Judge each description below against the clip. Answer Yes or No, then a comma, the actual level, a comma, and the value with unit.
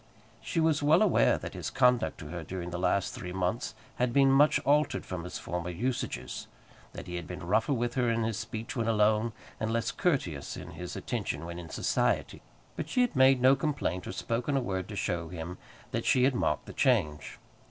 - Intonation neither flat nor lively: No, wide, 6.8 semitones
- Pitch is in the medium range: No, low, 115 Hz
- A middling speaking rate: No, fast, 210 wpm